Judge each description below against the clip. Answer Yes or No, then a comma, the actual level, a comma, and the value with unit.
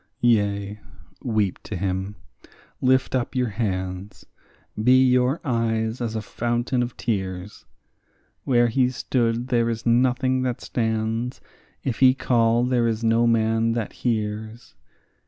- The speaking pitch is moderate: No, low, 115 Hz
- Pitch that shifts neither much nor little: No, narrow, 2.3 semitones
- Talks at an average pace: No, slow, 130 wpm